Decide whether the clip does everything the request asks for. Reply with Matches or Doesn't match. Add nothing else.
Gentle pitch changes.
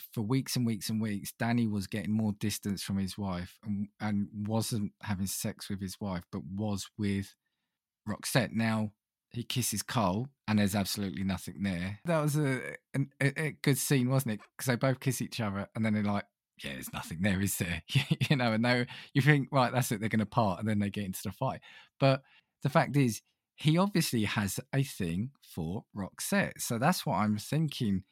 Doesn't match